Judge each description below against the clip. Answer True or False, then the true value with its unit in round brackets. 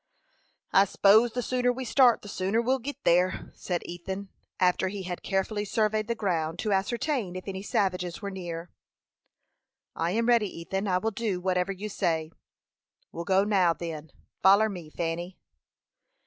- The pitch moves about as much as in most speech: True (3.3 semitones)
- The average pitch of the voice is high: True (195 Hz)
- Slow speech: False (160 wpm)